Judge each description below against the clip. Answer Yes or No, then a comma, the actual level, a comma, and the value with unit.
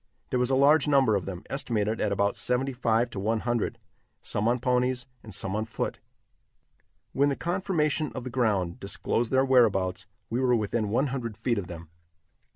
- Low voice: Yes, low, 120 Hz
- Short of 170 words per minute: No, average, 185 wpm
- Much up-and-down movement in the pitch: No, average, 4.1 semitones